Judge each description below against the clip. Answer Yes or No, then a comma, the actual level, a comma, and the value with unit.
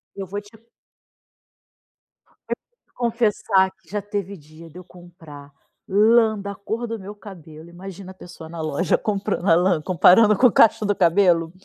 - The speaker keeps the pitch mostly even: No, average, 3.5 semitones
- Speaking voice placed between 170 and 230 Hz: Yes, high, 190 Hz